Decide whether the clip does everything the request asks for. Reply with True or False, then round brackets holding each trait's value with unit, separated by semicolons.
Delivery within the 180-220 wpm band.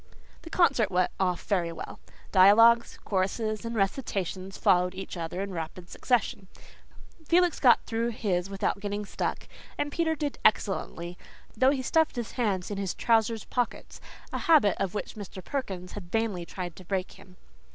False (160 wpm)